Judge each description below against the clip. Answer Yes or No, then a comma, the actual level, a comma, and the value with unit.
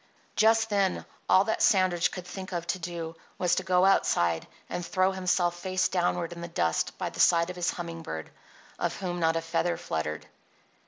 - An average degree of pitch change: No, narrow, 1.9 semitones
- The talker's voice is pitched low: No, medium, 175 Hz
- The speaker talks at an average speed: Yes, average, 195 wpm